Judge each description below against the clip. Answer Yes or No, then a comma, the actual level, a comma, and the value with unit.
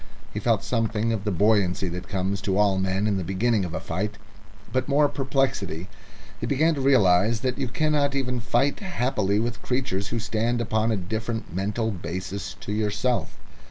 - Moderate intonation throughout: Yes, average, 4.3 semitones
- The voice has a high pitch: No, low, 110 Hz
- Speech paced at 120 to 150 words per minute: No, average, 180 wpm